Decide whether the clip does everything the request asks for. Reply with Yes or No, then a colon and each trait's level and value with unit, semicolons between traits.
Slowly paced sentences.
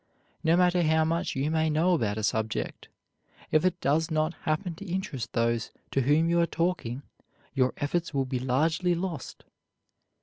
No: average, 170 wpm